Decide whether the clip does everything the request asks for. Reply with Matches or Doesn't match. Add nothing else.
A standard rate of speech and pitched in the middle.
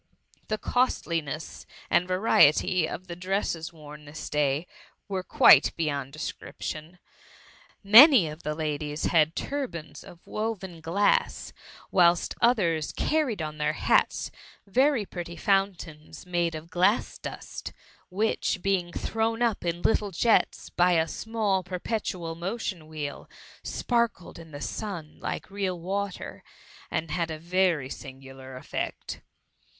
Doesn't match